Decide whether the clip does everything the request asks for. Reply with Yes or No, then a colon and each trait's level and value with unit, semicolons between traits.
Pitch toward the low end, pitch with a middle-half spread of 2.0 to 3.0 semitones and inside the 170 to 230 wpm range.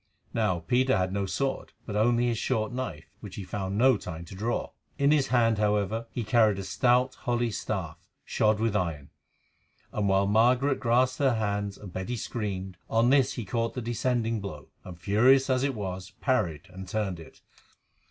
No: low, 110 Hz; average, 4.1 semitones; average, 180 wpm